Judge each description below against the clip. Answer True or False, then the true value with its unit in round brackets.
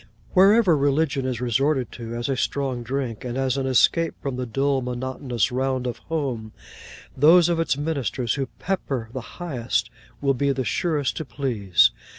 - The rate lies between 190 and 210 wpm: False (165 wpm)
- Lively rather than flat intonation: False (2.9 semitones)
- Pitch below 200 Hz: True (135 Hz)